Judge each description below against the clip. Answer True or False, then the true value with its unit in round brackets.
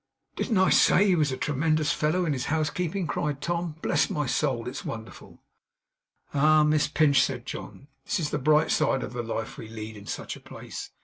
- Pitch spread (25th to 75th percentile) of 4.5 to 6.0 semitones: False (3.5 semitones)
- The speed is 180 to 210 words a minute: True (200 wpm)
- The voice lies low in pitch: False (150 Hz)